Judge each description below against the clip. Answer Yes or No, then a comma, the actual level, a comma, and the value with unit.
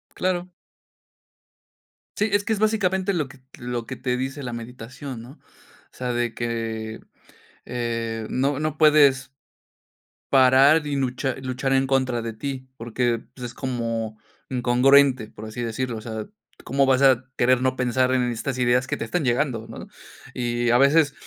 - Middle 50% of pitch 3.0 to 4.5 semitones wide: No, narrow, 2.6 semitones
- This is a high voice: No, low, 130 Hz